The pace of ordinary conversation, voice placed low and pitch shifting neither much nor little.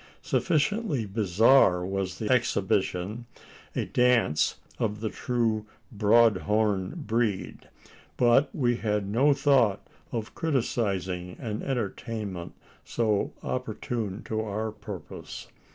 No: slow, 105 wpm; low, 110 Hz; average, 3.4 semitones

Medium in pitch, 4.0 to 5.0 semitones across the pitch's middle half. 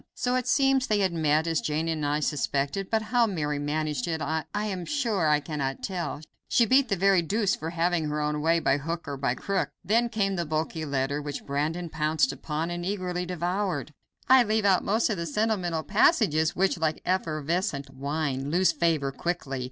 Yes: medium, 165 Hz; average, 4.6 semitones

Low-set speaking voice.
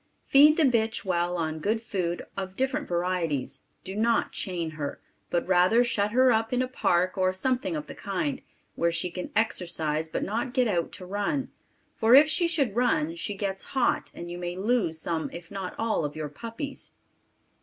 No: high, 195 Hz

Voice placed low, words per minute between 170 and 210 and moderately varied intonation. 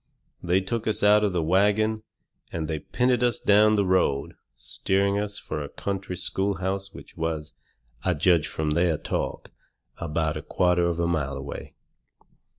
No: very low, 90 Hz; average, 160 wpm; average, 4.2 semitones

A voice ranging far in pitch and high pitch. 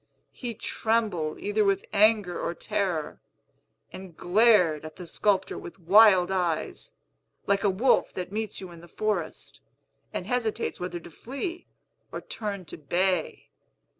No: average, 3.6 semitones; high, 195 Hz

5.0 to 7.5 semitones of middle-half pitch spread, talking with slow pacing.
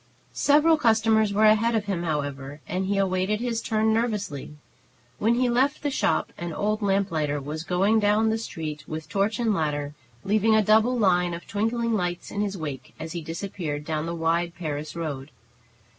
No: wide, 5.4 semitones; average, 180 wpm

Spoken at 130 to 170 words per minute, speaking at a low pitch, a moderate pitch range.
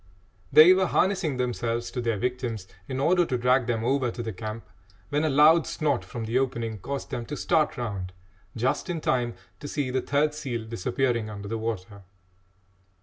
No: average, 185 wpm; low, 125 Hz; average, 3.9 semitones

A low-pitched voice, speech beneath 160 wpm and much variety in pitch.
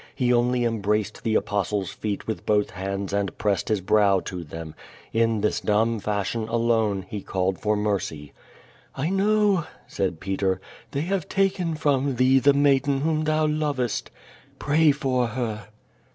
Yes: low, 115 Hz; average, 150 wpm; wide, 5.7 semitones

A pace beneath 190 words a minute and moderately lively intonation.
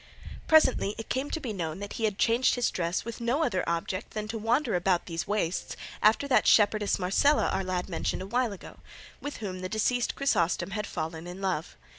No: fast, 205 wpm; average, 4.4 semitones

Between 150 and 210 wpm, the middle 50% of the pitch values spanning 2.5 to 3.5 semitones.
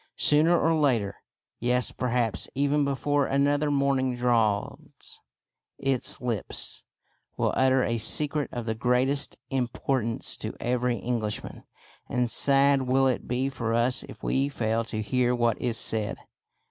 No: slow, 135 wpm; average, 2.8 semitones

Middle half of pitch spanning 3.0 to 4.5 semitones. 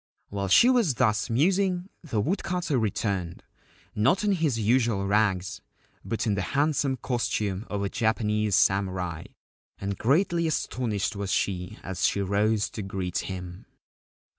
No: wide, 5.5 semitones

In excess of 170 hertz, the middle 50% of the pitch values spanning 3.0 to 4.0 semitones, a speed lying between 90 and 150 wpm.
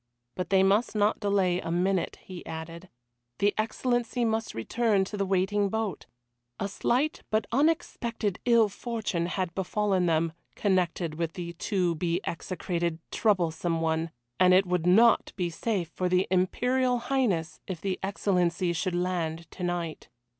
Yes: medium, 185 Hz; average, 3.7 semitones; average, 145 wpm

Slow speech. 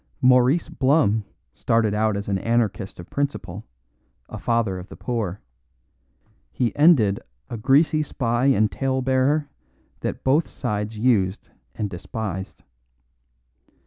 Yes: slow, 120 wpm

